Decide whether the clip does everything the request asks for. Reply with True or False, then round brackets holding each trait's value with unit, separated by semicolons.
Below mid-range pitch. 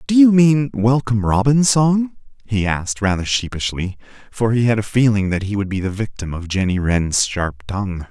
True (110 Hz)